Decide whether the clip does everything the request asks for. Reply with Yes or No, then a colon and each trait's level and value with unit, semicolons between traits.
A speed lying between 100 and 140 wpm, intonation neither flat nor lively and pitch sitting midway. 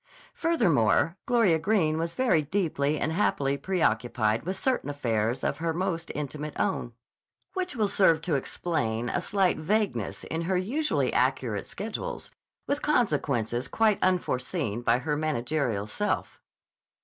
No: slow, 135 wpm; wide, 7.2 semitones; medium, 160 Hz